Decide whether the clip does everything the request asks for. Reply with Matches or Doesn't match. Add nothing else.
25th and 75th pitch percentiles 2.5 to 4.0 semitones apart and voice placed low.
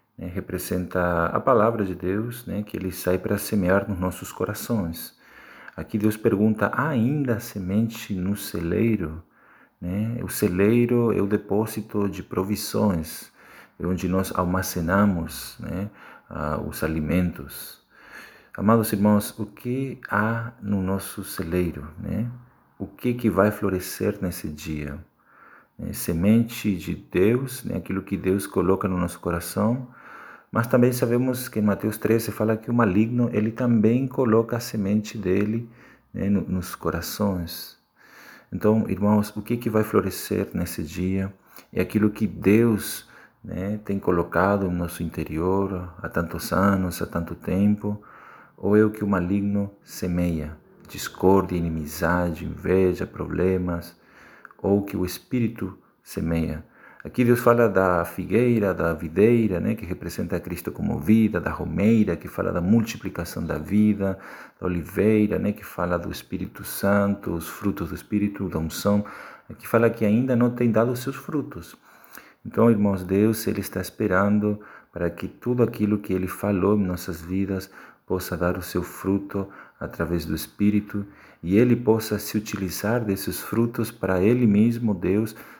Matches